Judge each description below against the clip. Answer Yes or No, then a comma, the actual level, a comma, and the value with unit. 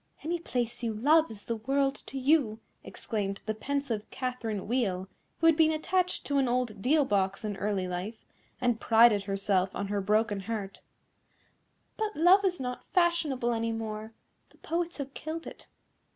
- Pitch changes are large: Yes, wide, 5.7 semitones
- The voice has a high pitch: Yes, high, 235 Hz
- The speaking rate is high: No, average, 165 wpm